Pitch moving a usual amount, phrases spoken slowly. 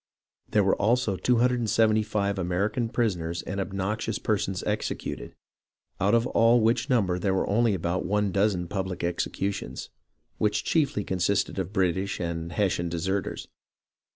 Yes: average, 3.0 semitones; slow, 130 wpm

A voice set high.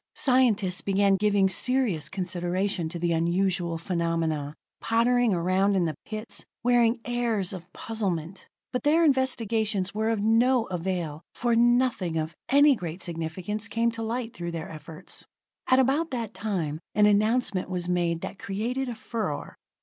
Yes: high, 200 Hz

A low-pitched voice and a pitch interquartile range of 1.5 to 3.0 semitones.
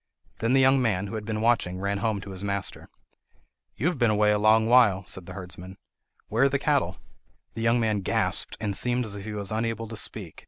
Yes: low, 110 Hz; average, 2.7 semitones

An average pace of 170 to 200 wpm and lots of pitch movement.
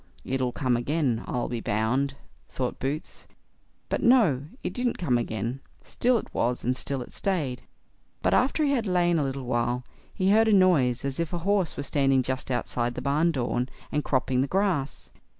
Yes: average, 185 wpm; wide, 6.0 semitones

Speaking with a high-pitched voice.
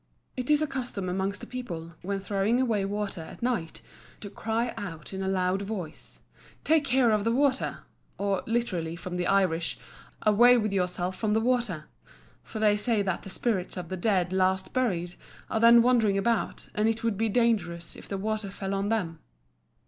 Yes: high, 200 Hz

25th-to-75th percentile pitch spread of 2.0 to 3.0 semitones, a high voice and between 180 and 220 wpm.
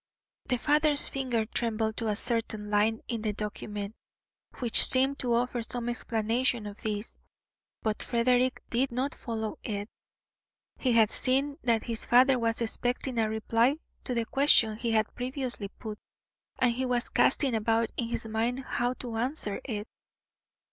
No: narrow, 2.5 semitones; high, 235 Hz; average, 155 wpm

